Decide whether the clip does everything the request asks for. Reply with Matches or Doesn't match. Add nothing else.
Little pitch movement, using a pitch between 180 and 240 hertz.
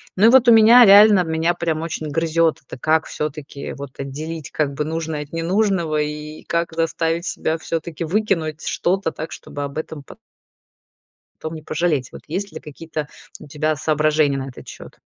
Doesn't match